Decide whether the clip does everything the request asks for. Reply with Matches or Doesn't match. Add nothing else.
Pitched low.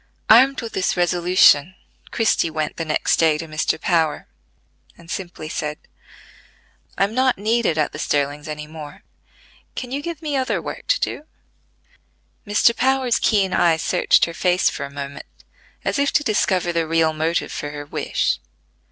Doesn't match